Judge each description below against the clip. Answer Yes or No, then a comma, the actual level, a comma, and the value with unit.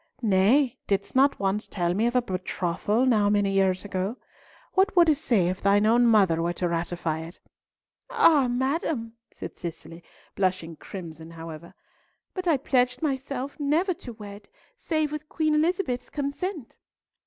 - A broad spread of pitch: Yes, wide, 7.2 semitones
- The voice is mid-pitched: No, high, 225 Hz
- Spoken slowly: No, average, 150 wpm